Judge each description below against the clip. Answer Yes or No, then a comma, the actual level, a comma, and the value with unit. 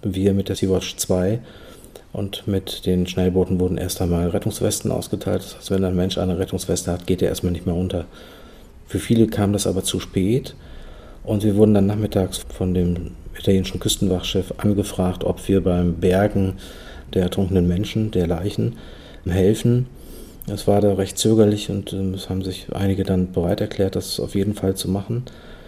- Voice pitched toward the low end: Yes, very low, 95 Hz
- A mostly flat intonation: Yes, narrow, 2.1 semitones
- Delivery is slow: No, average, 175 wpm